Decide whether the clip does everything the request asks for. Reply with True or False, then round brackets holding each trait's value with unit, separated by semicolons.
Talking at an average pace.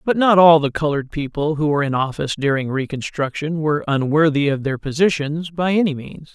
True (190 wpm)